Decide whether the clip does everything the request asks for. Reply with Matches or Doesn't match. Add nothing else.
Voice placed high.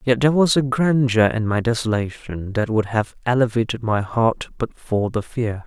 Doesn't match